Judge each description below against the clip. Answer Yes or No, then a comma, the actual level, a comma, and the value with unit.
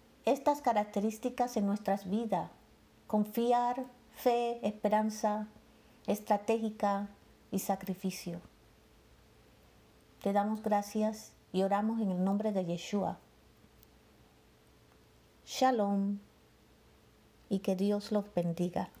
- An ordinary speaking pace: No, slow, 85 wpm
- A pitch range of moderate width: No, narrow, 2.0 semitones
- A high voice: Yes, high, 210 Hz